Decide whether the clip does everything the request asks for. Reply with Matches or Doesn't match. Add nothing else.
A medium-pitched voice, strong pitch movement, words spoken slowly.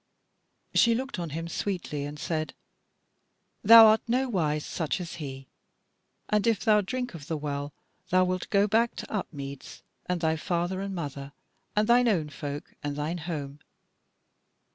Doesn't match